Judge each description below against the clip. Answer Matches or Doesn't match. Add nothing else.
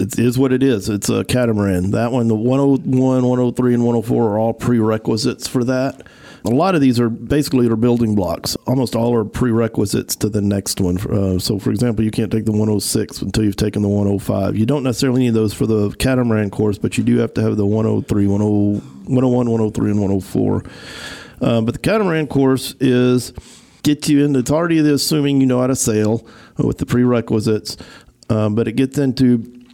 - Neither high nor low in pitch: Doesn't match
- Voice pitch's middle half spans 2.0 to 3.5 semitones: Matches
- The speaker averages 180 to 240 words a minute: Matches